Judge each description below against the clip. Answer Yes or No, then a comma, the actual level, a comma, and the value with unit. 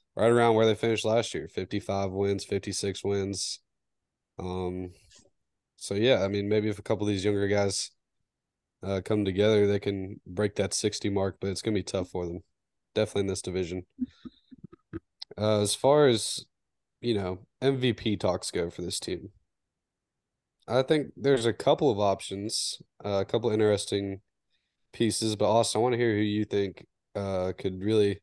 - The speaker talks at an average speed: Yes, average, 175 wpm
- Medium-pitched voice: No, low, 100 Hz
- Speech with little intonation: Yes, narrow, 1.9 semitones